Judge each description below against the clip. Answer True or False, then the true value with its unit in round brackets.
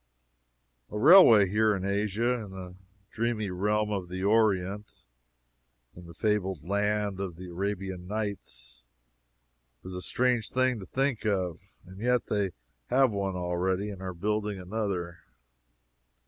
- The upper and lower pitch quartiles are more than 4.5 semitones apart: False (2.6 semitones)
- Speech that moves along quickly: False (135 wpm)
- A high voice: False (100 Hz)